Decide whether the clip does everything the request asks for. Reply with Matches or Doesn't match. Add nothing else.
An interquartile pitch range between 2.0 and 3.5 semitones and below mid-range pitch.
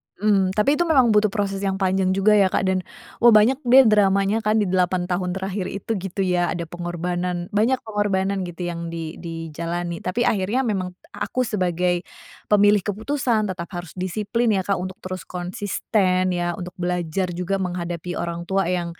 Doesn't match